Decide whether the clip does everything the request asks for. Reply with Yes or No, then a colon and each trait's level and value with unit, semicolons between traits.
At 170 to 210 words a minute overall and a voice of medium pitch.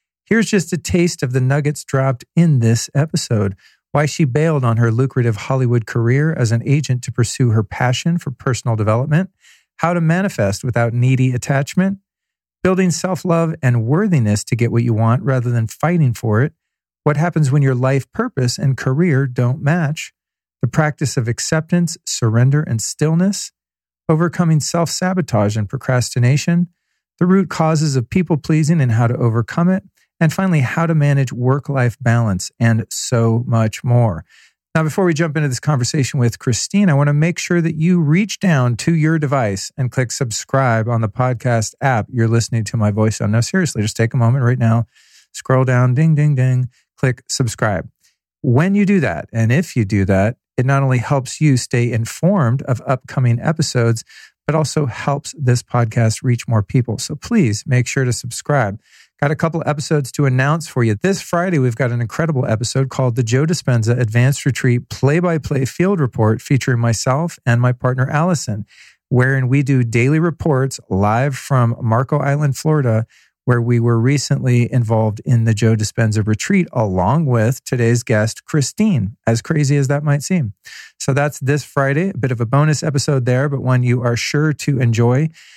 No: average, 180 wpm; low, 130 Hz